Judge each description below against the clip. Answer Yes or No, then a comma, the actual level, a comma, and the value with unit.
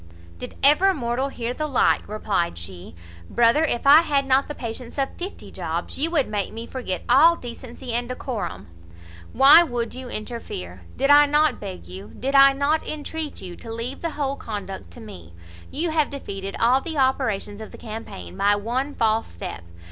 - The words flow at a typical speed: Yes, average, 185 wpm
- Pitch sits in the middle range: No, high, 245 Hz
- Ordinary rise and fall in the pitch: Yes, average, 5.0 semitones